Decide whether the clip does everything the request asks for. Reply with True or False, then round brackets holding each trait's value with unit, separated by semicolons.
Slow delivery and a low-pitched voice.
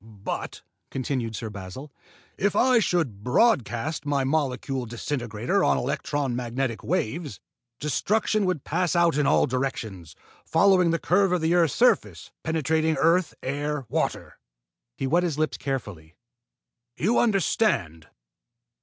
False (130 wpm; 145 Hz)